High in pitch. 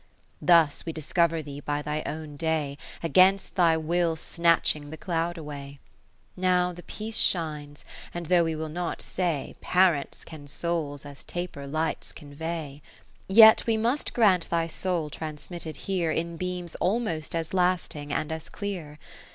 No: medium, 165 Hz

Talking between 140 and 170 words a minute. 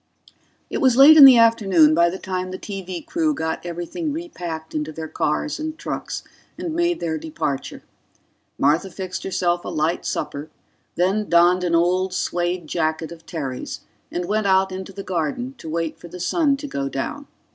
No: average, 180 wpm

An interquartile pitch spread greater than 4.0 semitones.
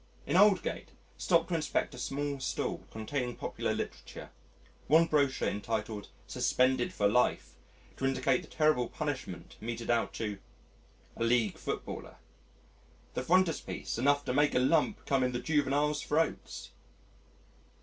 No: average, 3.7 semitones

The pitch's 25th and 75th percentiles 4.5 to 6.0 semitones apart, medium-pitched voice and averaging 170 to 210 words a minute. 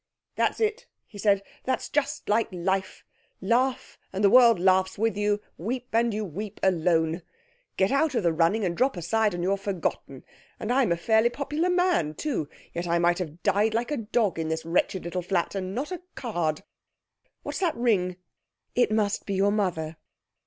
No: average, 5.2 semitones; high, 200 Hz; average, 185 wpm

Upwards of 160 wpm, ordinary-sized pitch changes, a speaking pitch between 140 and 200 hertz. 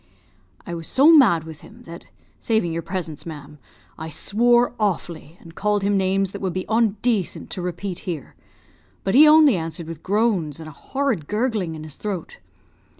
Yes: average, 175 wpm; average, 5.0 semitones; high, 190 Hz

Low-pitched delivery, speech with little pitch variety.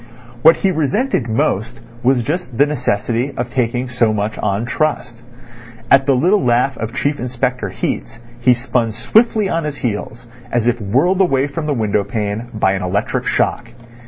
No: low, 125 Hz; average, 4.0 semitones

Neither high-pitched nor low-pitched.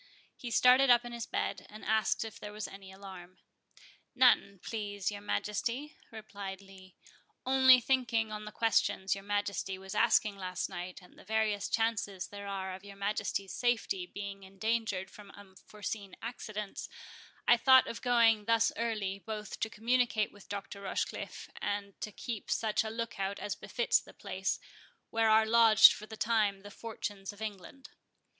No: high, 210 Hz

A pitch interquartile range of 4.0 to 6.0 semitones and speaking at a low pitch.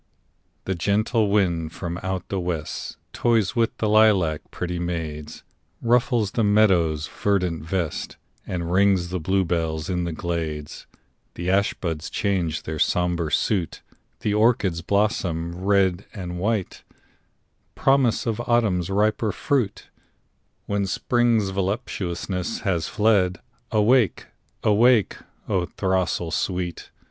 No: average, 3.5 semitones; very low, 95 Hz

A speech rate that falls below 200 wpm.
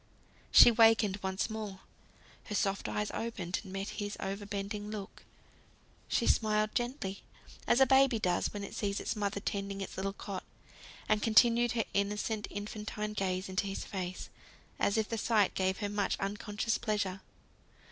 Yes: average, 160 wpm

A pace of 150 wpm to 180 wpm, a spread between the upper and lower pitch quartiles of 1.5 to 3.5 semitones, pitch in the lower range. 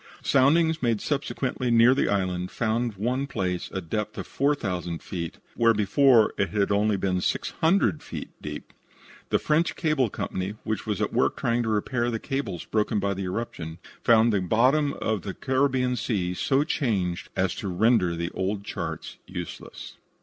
No: average, 170 wpm; wide, 5.5 semitones; low, 110 Hz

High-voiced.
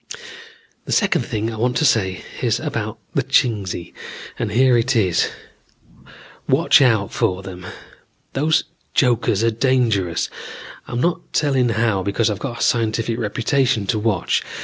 No: low, 115 Hz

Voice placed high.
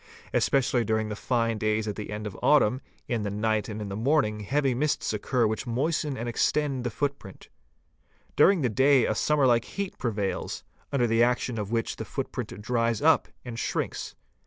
No: low, 115 Hz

